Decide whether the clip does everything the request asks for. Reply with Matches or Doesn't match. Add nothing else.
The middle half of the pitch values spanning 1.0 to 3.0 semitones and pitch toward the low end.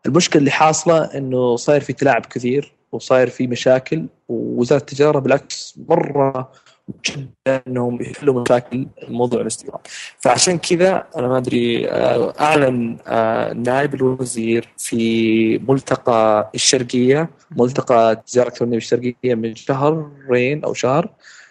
Matches